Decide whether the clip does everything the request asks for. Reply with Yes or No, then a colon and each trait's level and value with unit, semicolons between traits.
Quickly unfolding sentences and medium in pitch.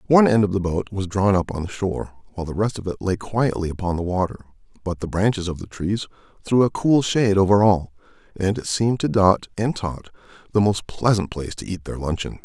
No: fast, 230 wpm; very low, 95 Hz